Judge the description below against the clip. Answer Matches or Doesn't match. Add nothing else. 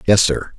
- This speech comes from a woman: Doesn't match